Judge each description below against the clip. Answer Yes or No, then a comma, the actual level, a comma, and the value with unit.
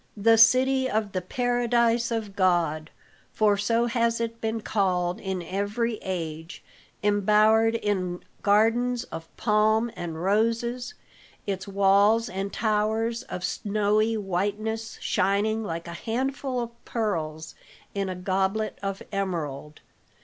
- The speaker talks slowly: Yes, slow, 120 wpm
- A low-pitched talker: No, high, 210 Hz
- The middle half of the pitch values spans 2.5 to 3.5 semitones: Yes, average, 3.2 semitones